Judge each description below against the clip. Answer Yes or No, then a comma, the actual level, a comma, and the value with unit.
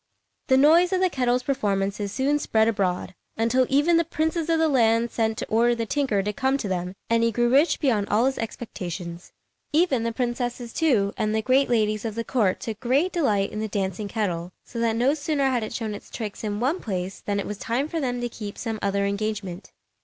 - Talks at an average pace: No, fast, 220 wpm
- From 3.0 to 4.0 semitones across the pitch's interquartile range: No, average, 4.4 semitones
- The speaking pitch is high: Yes, high, 230 Hz